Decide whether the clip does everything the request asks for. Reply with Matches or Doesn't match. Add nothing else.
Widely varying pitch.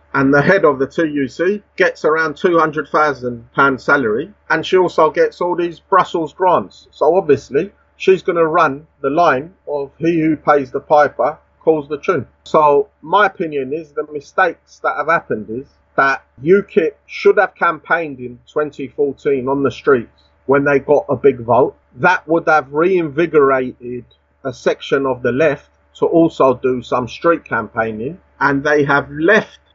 Doesn't match